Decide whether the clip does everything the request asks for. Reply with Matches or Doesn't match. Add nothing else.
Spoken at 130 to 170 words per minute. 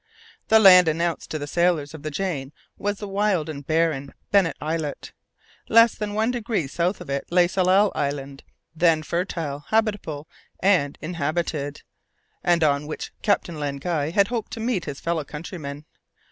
Matches